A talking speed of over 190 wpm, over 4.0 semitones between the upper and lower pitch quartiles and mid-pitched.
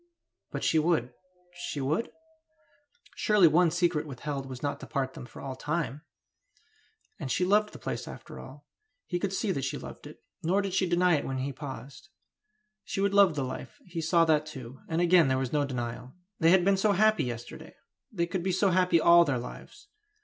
Yes: average, 200 wpm; average, 5.2 semitones; medium, 160 Hz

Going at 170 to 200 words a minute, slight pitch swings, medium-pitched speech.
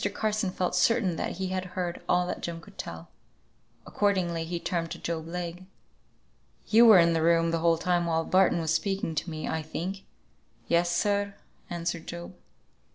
Yes: average, 175 wpm; narrow, 2.0 semitones; medium, 175 Hz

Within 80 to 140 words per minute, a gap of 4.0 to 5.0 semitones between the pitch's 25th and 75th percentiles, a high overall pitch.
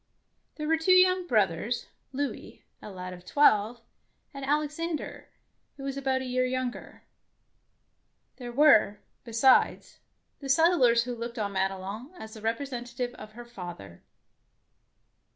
Yes: slow, 135 wpm; average, 4.5 semitones; high, 245 Hz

